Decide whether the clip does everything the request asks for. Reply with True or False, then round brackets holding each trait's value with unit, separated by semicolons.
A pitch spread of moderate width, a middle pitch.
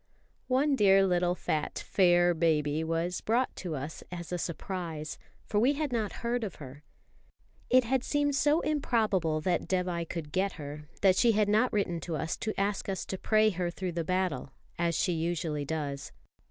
True (4.9 semitones; 180 Hz)